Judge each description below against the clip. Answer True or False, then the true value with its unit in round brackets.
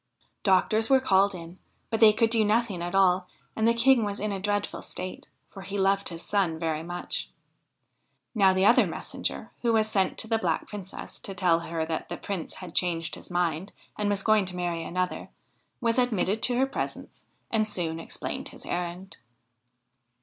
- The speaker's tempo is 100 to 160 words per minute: False (185 wpm)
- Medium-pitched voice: False (195 Hz)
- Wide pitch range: False (3.6 semitones)